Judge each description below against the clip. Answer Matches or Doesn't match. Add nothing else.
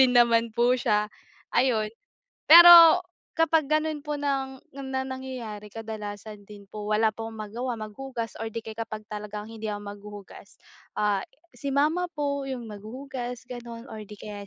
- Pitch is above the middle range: Matches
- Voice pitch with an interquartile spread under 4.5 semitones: Matches